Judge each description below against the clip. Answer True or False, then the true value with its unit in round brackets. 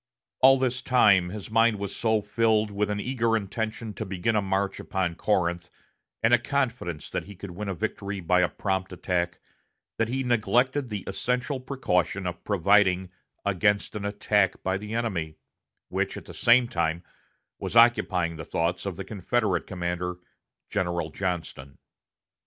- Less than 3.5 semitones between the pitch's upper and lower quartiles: False (4.0 semitones)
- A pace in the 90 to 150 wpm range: False (160 wpm)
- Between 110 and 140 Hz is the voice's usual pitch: False (100 Hz)